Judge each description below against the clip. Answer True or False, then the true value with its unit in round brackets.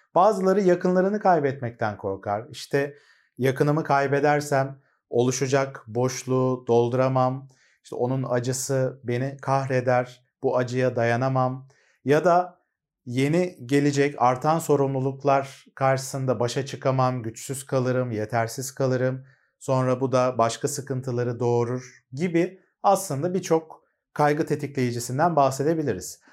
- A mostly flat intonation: True (2.2 semitones)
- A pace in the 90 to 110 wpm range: True (100 wpm)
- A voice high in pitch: False (135 Hz)